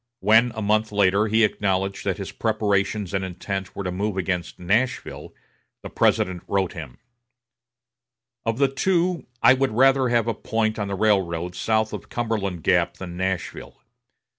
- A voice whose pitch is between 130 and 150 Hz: No, low, 105 Hz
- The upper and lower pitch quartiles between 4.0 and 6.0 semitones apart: No, average, 3.0 semitones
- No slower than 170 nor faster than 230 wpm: No, average, 160 wpm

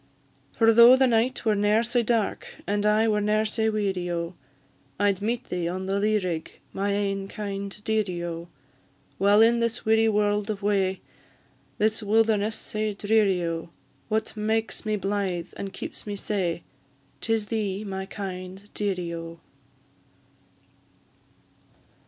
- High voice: Yes, high, 205 Hz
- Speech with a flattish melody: Yes, narrow, 2.3 semitones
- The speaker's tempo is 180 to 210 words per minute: No, average, 145 wpm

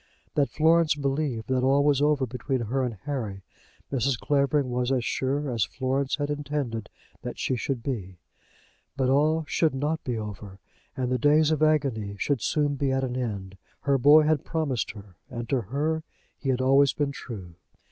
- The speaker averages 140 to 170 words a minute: No, average, 180 wpm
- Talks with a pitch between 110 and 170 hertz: Yes, low, 135 Hz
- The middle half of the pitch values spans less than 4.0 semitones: Yes, average, 3.4 semitones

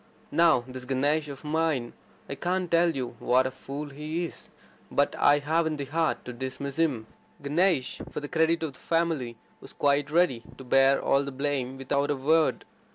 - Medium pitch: Yes, medium, 145 Hz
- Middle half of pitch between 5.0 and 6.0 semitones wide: No, average, 3.3 semitones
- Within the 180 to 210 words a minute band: Yes, average, 185 wpm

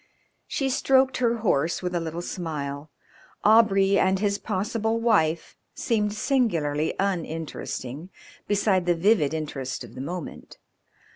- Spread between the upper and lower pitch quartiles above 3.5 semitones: Yes, wide, 5.5 semitones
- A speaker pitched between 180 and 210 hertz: Yes, medium, 185 Hz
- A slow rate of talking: Yes, slow, 125 wpm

